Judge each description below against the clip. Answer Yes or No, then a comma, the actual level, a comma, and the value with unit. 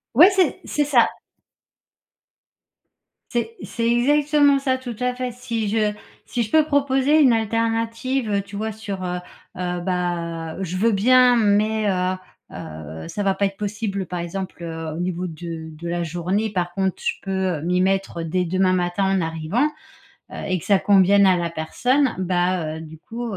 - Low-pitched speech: No, high, 195 Hz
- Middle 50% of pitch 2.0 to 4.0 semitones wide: No, average, 4.7 semitones